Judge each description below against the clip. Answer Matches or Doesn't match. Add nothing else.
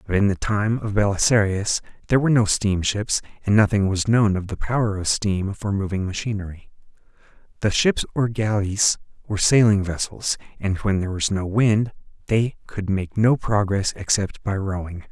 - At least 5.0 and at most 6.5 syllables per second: Matches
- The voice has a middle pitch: Doesn't match